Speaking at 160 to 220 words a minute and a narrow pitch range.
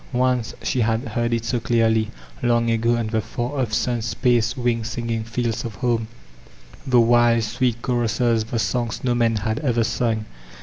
Yes: average, 180 wpm; narrow, 1.3 semitones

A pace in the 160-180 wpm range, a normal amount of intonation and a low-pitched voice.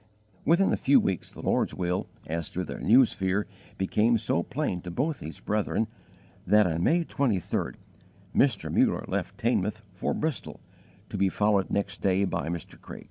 Yes: average, 170 wpm; average, 4.8 semitones; low, 100 Hz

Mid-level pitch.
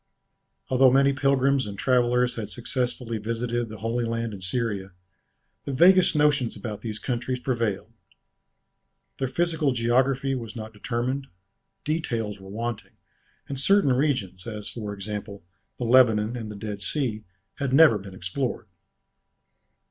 No: low, 120 Hz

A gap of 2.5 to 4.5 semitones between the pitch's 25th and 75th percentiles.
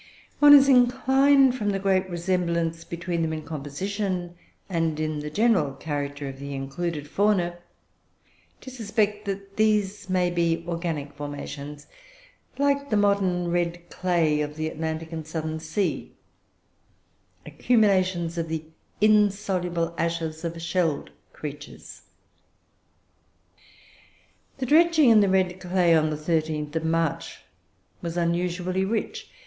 Yes: average, 4.1 semitones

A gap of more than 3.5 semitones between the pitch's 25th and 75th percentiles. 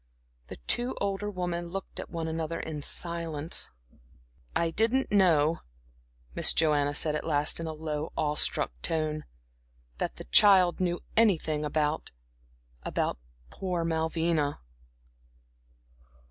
No: average, 2.8 semitones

